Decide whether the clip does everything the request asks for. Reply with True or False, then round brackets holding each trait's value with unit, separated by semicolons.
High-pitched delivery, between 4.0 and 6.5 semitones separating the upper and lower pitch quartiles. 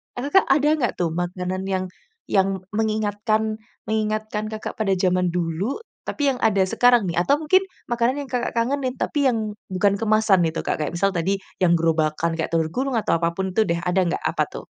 True (205 Hz; 4.6 semitones)